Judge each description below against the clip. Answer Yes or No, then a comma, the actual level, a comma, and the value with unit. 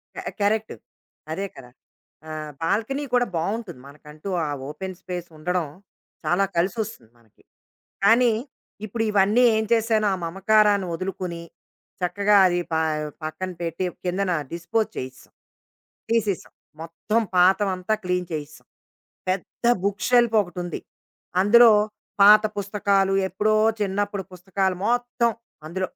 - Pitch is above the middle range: Yes, high, 195 Hz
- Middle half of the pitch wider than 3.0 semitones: Yes, average, 3.5 semitones